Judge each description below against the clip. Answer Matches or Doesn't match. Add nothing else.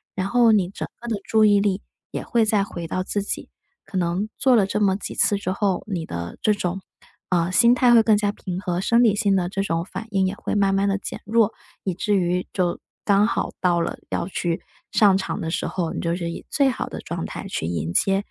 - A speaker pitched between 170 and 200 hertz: Matches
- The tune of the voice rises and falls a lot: Doesn't match